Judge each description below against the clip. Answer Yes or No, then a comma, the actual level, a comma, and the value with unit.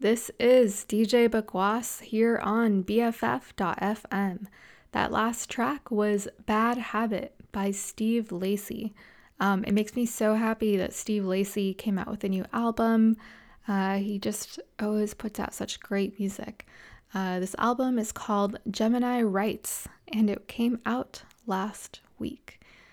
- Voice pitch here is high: Yes, high, 215 Hz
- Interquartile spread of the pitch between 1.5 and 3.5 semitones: Yes, narrow, 2.5 semitones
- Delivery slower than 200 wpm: Yes, average, 140 wpm